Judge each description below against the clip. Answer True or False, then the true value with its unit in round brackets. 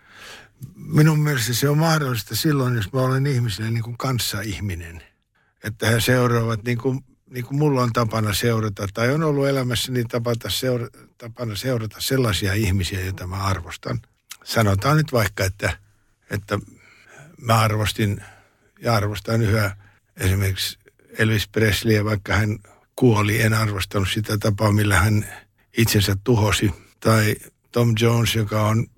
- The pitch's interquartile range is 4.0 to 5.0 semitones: False (3.0 semitones)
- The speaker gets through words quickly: False (135 wpm)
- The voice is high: False (110 Hz)